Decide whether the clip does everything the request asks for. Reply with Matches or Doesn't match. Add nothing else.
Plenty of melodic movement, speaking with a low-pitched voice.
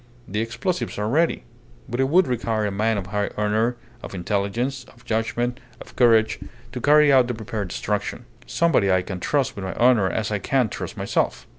Doesn't match